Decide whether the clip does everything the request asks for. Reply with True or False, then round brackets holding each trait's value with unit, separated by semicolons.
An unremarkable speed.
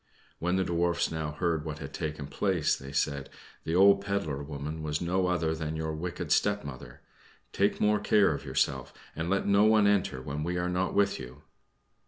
True (190 wpm)